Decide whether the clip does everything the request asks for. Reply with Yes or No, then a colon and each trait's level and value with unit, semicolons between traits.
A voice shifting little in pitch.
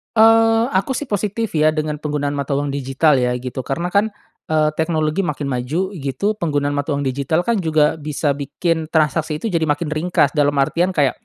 No: average, 3.6 semitones